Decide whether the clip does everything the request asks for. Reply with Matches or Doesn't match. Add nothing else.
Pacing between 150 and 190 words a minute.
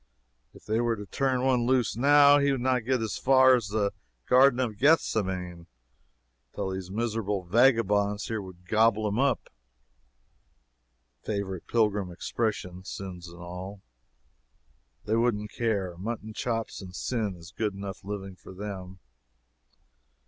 Doesn't match